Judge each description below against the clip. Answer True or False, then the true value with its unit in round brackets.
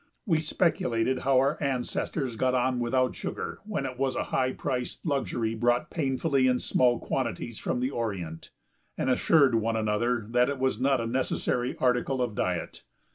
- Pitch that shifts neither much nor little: False (2.2 semitones)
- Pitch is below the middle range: True (125 Hz)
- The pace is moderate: True (170 wpm)